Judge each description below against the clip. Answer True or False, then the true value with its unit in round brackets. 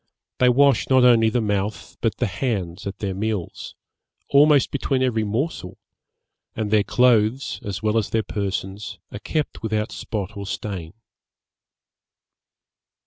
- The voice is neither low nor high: False (110 Hz)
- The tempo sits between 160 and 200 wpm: False (140 wpm)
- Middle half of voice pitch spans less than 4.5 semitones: True (3.7 semitones)